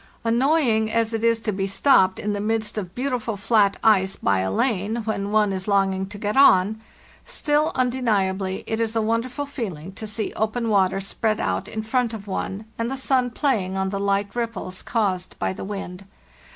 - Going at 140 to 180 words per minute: No, average, 190 wpm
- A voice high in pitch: Yes, high, 215 Hz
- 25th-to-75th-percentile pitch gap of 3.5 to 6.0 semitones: No, average, 3.0 semitones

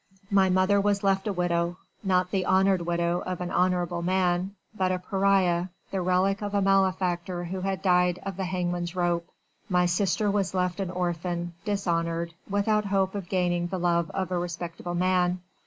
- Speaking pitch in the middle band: Yes, medium, 180 Hz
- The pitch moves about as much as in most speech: No, narrow, 1.7 semitones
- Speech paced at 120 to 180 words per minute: Yes, average, 175 wpm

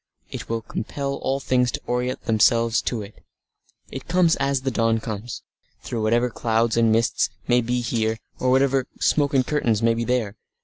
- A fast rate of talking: No, average, 180 wpm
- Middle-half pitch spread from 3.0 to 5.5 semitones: No, narrow, 2.5 semitones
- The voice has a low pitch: Yes, low, 120 Hz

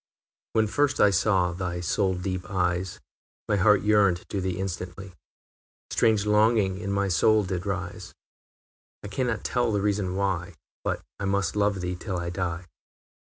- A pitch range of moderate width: No, narrow, 2.3 semitones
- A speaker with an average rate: Yes, average, 160 wpm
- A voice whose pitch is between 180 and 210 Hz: No, very low, 95 Hz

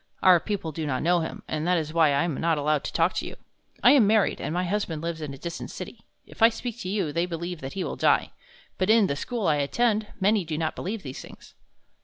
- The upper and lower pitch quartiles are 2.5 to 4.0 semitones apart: No, average, 4.6 semitones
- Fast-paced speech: Yes, fast, 260 wpm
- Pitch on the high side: No, medium, 170 Hz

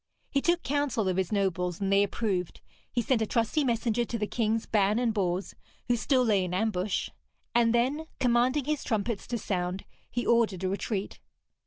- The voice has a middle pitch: No, high, 220 Hz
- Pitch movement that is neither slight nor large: Yes, average, 3.8 semitones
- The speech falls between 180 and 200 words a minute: Yes, average, 185 wpm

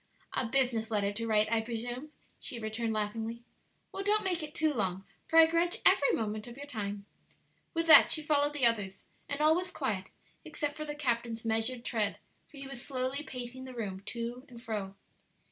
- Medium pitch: No, high, 240 Hz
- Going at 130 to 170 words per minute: No, average, 195 wpm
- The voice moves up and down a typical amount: Yes, average, 4.9 semitones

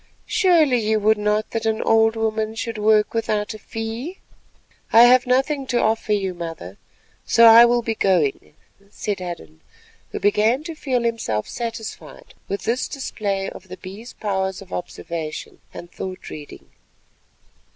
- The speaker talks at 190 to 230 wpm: No, average, 150 wpm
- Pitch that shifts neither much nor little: Yes, average, 3.4 semitones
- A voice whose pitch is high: Yes, high, 220 Hz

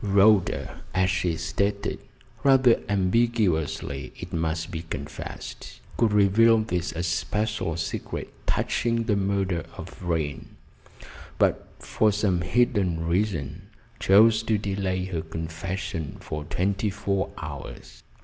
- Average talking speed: No, slow, 110 wpm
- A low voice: Yes, very low, 95 Hz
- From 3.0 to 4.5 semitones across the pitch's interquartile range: Yes, average, 4.1 semitones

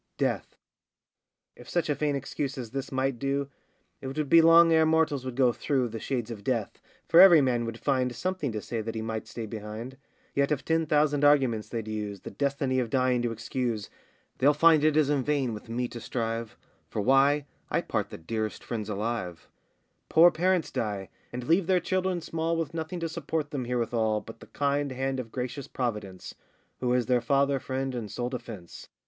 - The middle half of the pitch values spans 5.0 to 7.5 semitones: No, average, 4.3 semitones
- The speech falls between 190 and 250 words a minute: Yes, average, 200 wpm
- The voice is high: No, low, 130 Hz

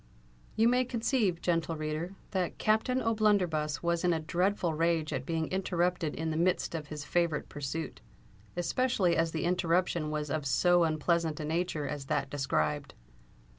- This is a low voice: No, medium, 165 Hz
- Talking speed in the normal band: Yes, average, 155 wpm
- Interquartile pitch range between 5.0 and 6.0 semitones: No, average, 2.9 semitones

